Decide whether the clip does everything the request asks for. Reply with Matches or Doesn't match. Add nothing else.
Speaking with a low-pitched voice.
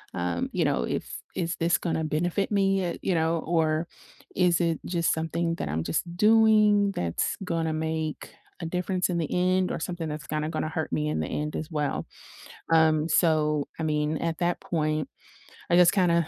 Doesn't match